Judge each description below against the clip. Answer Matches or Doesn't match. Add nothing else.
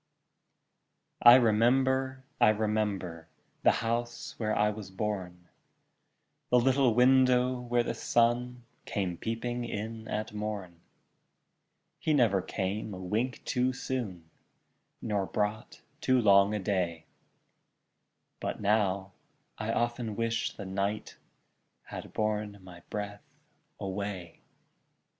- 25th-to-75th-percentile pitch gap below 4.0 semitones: Matches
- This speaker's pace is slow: Matches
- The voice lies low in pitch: Matches